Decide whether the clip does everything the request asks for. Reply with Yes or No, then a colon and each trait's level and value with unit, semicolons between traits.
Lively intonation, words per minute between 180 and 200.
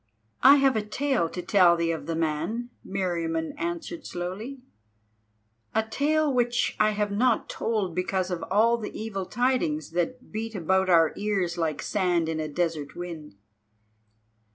No: wide, 5.7 semitones; average, 155 wpm